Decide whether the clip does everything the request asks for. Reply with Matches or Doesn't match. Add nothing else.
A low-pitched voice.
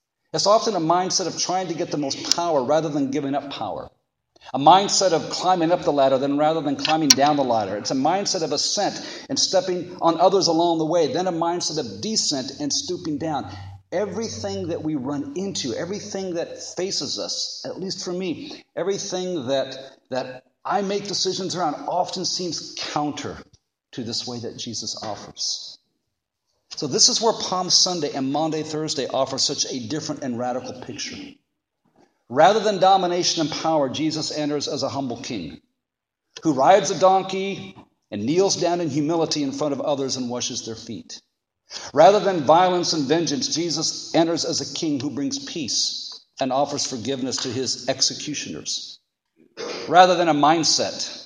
Doesn't match